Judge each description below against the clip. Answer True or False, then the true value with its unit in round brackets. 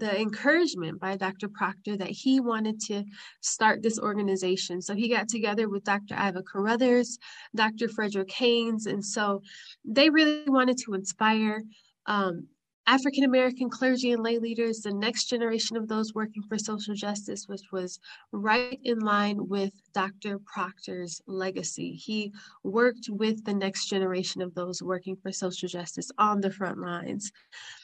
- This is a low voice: False (210 Hz)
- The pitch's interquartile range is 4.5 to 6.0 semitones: False (2.9 semitones)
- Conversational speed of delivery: True (155 wpm)